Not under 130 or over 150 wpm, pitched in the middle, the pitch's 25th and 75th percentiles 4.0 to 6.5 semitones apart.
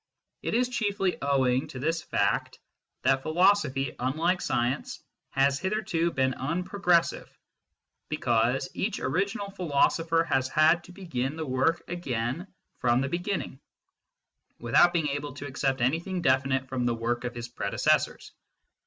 Yes: slow, 135 wpm; medium, 145 Hz; average, 5.1 semitones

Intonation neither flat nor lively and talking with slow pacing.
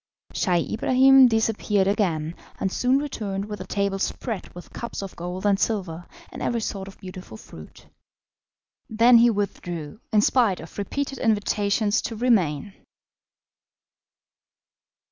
Yes: average, 3.6 semitones; slow, 130 wpm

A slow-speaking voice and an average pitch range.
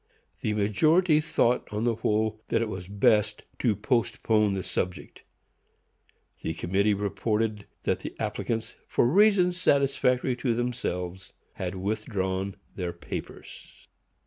Yes: slow, 120 wpm; average, 3.9 semitones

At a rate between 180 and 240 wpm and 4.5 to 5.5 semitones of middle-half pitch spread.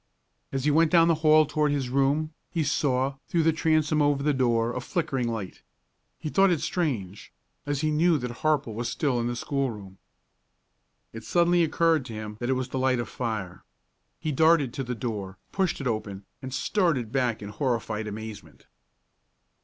Yes: average, 185 wpm; average, 5.0 semitones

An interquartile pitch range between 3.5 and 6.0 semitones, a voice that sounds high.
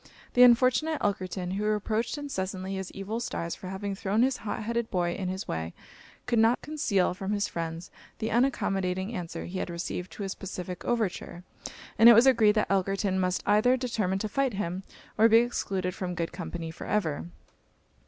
Yes: average, 3.8 semitones; high, 195 Hz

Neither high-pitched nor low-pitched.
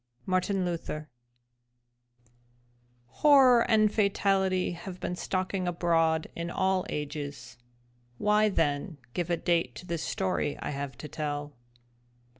Yes: medium, 175 Hz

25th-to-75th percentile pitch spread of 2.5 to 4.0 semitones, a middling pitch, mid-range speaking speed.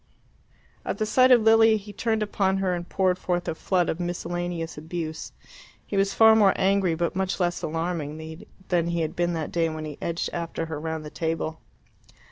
Yes: average, 3.1 semitones; medium, 175 Hz; average, 195 wpm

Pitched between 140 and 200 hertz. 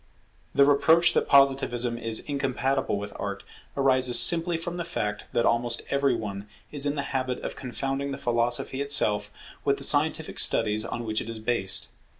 No: low, 125 Hz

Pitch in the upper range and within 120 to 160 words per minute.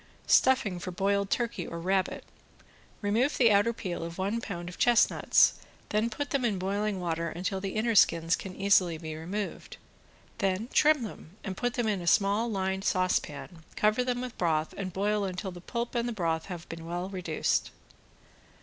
No: high, 195 Hz; average, 175 wpm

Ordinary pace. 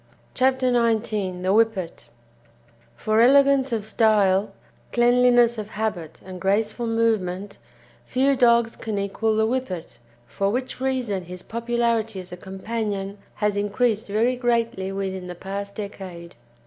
No: slow, 130 wpm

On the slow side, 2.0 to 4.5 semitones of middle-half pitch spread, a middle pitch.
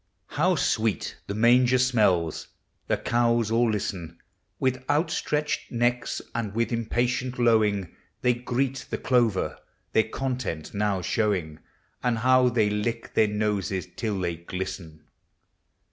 No: slow, 130 wpm; average, 3.7 semitones; low, 115 Hz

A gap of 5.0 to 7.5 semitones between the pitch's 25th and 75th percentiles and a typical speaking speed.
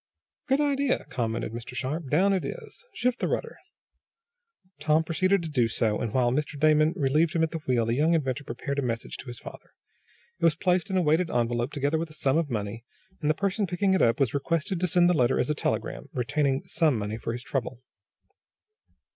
No: wide, 5.6 semitones; fast, 215 wpm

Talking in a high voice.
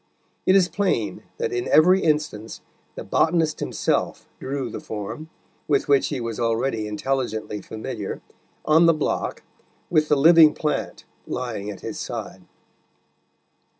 No: low, 135 Hz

